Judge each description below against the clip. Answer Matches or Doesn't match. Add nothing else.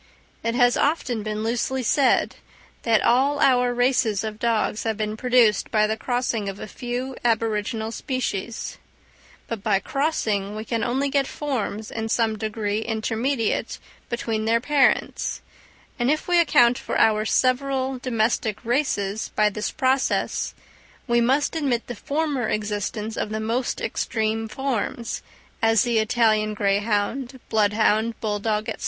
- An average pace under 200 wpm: Matches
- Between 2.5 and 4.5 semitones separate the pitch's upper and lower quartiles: Matches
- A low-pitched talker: Doesn't match